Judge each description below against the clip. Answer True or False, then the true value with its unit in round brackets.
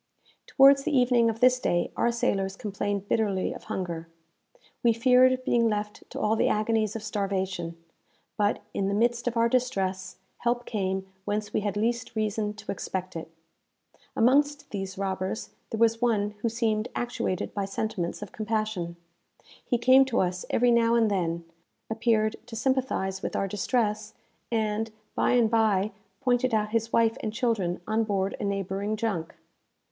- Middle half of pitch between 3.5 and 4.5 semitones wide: False (3.1 semitones)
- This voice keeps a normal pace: True (160 wpm)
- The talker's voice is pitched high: True (215 Hz)